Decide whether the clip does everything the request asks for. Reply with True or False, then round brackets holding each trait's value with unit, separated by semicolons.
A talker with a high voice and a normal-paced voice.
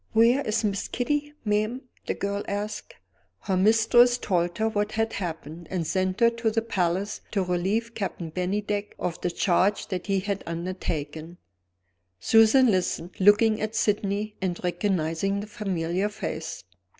True (200 Hz; 150 wpm)